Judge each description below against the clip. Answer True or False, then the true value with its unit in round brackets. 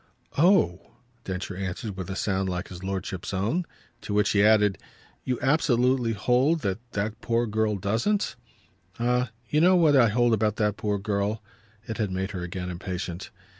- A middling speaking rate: True (170 wpm)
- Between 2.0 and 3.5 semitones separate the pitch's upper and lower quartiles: False (4.0 semitones)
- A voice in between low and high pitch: False (105 Hz)